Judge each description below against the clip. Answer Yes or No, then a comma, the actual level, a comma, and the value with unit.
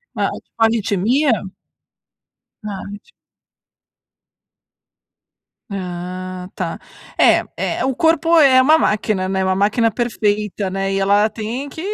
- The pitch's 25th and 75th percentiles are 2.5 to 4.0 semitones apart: No, average, 4.5 semitones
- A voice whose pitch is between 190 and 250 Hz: Yes, high, 210 Hz